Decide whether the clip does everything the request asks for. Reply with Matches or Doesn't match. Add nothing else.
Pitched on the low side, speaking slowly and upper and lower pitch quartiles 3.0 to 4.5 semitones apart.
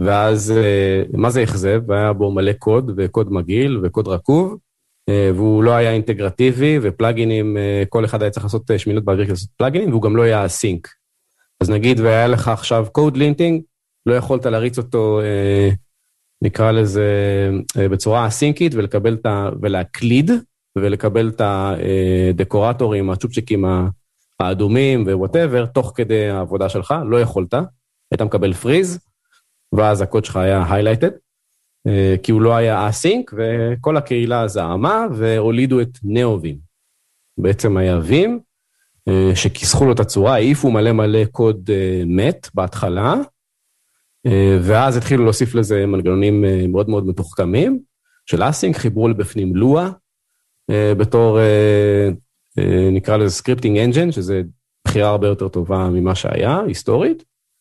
Doesn't match